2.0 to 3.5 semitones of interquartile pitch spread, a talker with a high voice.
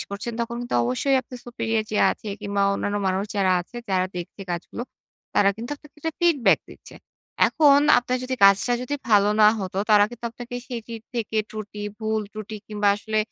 Yes: average, 3.2 semitones; high, 220 Hz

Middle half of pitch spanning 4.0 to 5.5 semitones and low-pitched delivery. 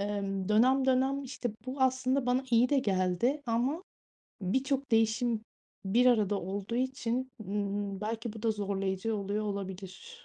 No: average, 4.4 semitones; high, 225 Hz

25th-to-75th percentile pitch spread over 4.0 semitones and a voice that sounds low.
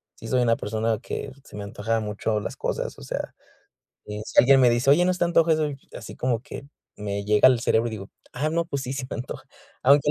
Yes: average, 4.5 semitones; low, 120 Hz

